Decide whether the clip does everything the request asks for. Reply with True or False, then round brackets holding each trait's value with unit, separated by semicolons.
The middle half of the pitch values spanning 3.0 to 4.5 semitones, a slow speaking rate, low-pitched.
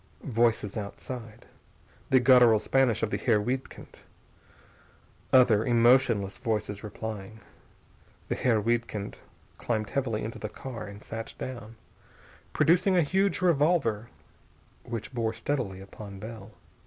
True (3.3 semitones; 115 wpm; 115 Hz)